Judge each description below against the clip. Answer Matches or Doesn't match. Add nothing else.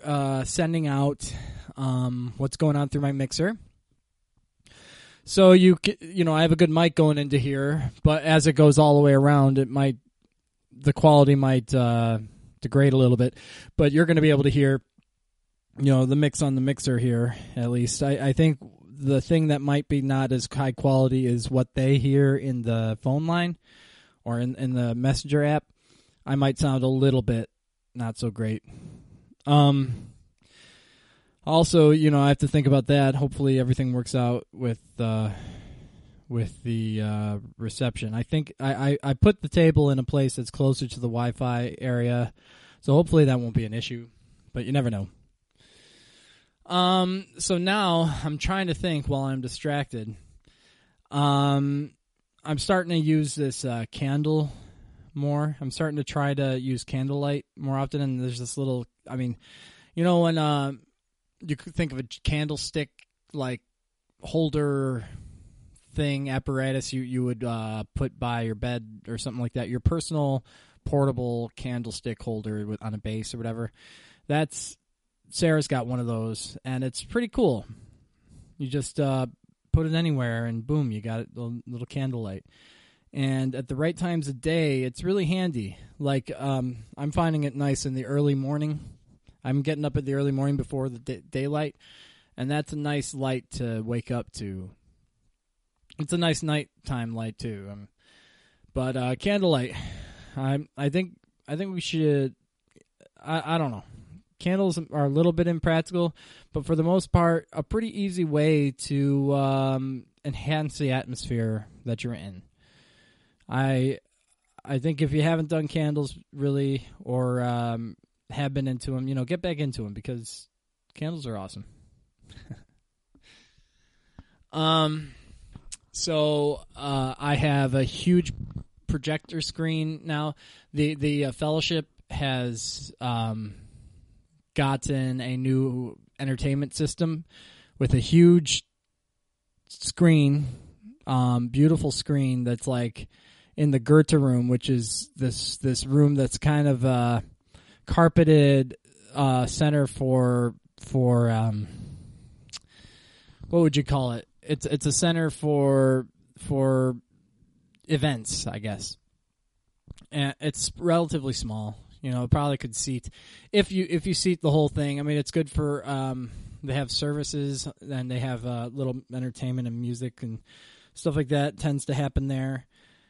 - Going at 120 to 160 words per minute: Matches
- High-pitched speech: Doesn't match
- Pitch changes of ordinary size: Matches